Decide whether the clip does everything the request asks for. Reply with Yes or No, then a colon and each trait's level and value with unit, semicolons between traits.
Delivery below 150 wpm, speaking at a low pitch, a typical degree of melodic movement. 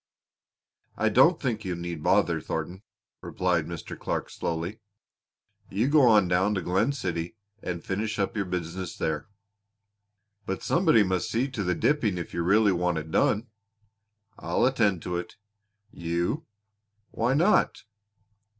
Yes: average, 140 wpm; very low, 95 Hz; average, 4.4 semitones